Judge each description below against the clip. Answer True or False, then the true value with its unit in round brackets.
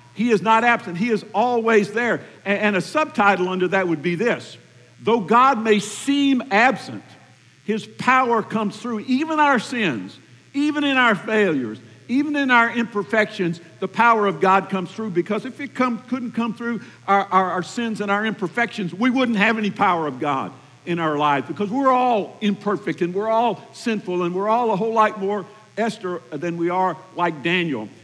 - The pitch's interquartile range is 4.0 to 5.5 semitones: True (4.3 semitones)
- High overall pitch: True (210 Hz)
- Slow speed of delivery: False (185 wpm)